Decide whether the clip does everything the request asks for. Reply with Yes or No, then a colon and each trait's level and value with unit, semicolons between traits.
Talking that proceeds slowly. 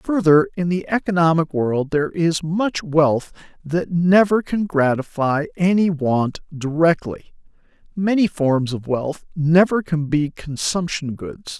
Yes: slow, 130 wpm